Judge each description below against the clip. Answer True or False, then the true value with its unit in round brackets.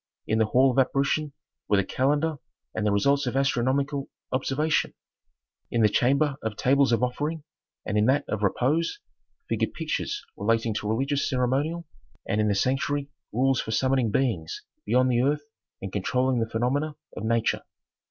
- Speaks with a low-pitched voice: True (130 Hz)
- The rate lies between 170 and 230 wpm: False (160 wpm)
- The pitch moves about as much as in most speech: True (3.9 semitones)